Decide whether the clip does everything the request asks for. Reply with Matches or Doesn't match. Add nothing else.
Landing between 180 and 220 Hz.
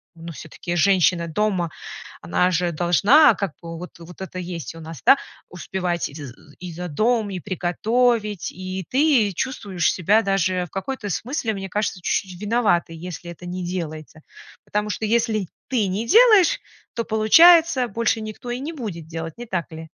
Matches